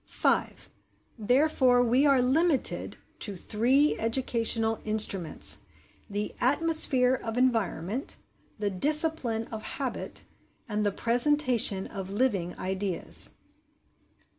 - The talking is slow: Yes, slow, 95 wpm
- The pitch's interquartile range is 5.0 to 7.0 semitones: No, average, 4.2 semitones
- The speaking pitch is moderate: No, high, 235 Hz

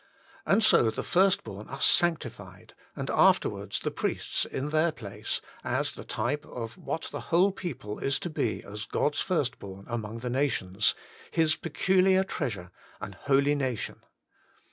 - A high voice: No, low, 135 Hz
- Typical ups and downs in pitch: No, wide, 7.5 semitones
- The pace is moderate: Yes, average, 160 wpm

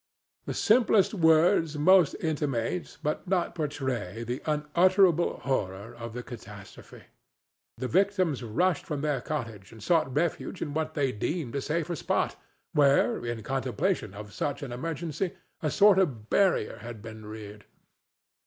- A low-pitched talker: No, medium, 145 Hz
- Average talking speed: Yes, average, 145 wpm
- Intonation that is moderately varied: No, wide, 6.3 semitones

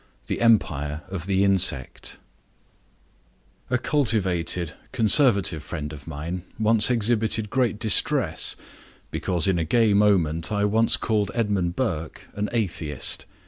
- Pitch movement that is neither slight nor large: Yes, average, 4.9 semitones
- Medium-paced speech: No, slow, 120 wpm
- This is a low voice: Yes, low, 100 Hz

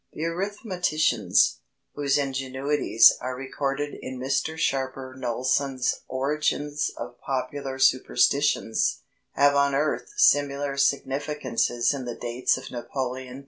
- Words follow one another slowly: Yes, slow, 105 wpm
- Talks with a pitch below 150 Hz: Yes, low, 135 Hz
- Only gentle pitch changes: Yes, narrow, 2.0 semitones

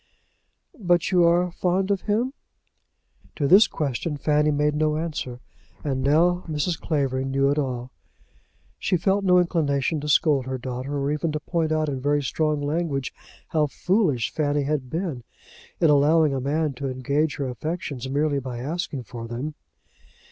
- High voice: No, medium, 150 Hz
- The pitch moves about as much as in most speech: Yes, average, 3.3 semitones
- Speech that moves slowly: No, average, 160 wpm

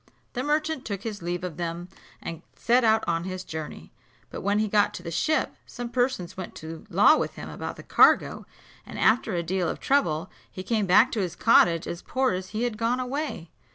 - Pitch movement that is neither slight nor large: No, wide, 6.0 semitones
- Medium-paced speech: No, fast, 215 wpm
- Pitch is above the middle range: Yes, high, 200 Hz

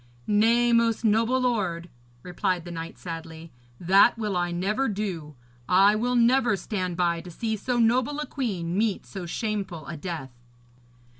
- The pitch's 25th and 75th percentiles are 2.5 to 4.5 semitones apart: No, average, 5.0 semitones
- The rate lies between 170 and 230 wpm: No, average, 155 wpm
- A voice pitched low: No, high, 200 Hz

